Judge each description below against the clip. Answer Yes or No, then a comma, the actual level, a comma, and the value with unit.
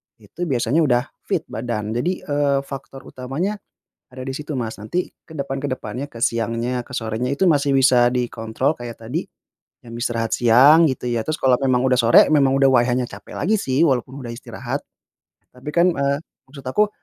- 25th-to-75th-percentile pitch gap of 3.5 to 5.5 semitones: No, average, 3.1 semitones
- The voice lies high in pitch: No, low, 130 Hz